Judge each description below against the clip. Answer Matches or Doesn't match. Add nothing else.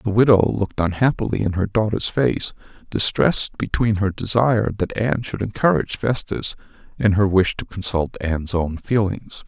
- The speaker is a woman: Doesn't match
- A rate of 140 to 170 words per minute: Matches